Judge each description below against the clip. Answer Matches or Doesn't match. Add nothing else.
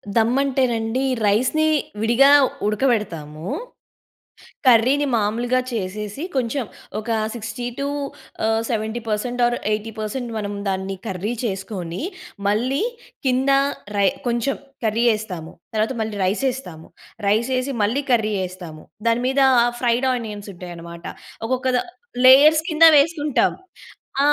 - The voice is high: Matches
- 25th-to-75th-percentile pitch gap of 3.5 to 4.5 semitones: Matches